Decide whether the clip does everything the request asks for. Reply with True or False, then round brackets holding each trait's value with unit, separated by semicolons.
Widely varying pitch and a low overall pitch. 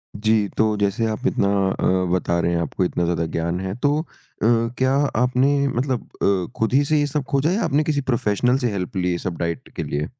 True (7.0 semitones; 110 Hz)